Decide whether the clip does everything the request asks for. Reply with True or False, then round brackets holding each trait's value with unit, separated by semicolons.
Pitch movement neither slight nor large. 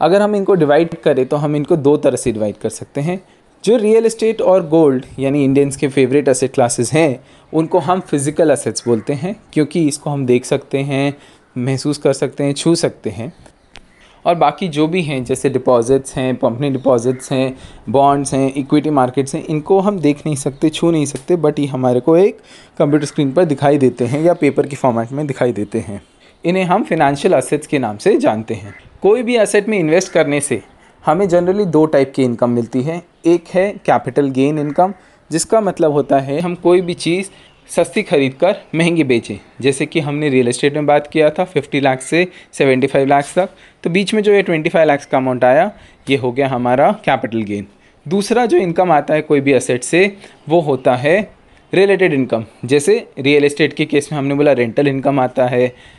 True (4.4 semitones)